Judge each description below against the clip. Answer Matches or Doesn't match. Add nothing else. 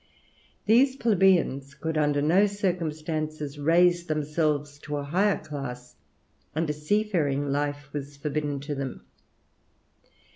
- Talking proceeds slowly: Matches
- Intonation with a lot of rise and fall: Doesn't match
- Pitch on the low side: Doesn't match